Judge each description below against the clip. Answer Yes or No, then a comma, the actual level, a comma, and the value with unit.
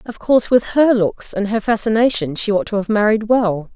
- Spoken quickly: Yes, fast, 225 wpm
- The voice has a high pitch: Yes, high, 215 Hz